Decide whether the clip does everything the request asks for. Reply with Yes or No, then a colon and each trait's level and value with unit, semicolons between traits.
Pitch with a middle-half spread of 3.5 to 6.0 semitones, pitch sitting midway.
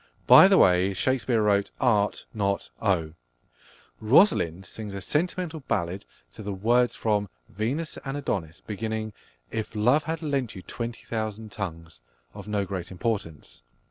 No: average, 4.1 semitones; low, 105 Hz